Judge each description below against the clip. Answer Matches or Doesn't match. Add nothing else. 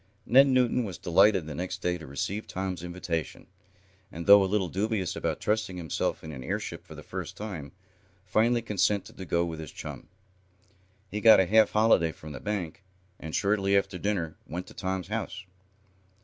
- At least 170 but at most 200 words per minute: Matches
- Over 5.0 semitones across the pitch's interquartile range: Doesn't match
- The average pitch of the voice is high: Doesn't match